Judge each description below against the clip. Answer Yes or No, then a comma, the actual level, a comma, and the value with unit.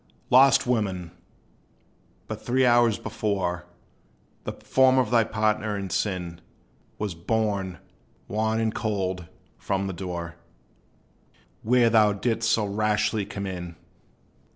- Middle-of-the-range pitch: No, low, 105 Hz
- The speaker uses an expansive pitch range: No, average, 3.2 semitones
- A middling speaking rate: No, slow, 115 wpm